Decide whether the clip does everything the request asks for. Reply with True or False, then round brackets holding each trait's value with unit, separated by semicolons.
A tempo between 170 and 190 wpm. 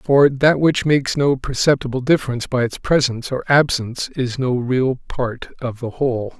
True (180 wpm)